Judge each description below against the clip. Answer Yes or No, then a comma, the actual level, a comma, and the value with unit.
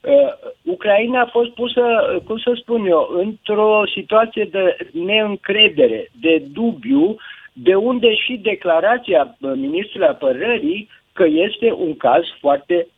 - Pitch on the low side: No, high, 225 Hz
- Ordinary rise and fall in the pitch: Yes, average, 4.4 semitones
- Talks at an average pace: Yes, average, 125 wpm